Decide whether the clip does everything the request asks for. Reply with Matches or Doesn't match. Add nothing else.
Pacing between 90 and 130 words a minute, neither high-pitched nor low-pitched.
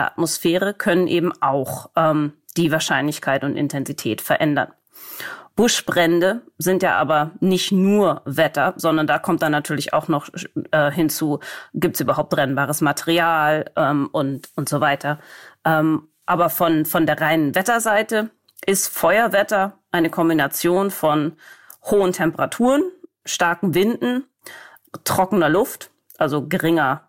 Matches